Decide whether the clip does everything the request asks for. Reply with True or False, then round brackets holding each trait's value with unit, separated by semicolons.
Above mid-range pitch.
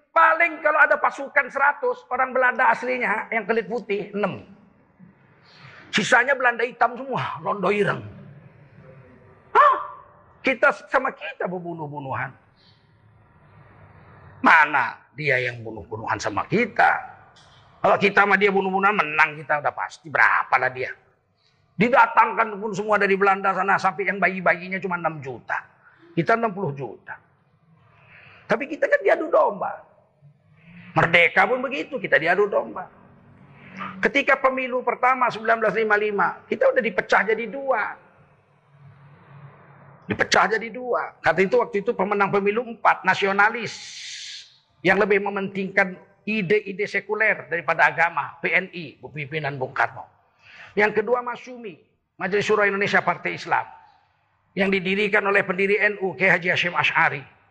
True (200 Hz)